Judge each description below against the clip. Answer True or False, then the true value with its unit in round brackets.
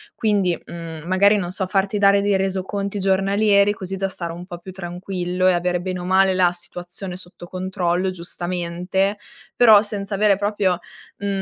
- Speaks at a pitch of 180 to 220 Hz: True (190 Hz)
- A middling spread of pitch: False (2.0 semitones)